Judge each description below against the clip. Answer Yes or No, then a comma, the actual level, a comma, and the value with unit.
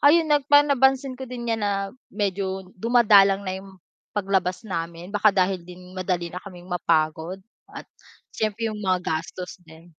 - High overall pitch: Yes, high, 195 Hz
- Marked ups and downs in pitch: No, average, 3.3 semitones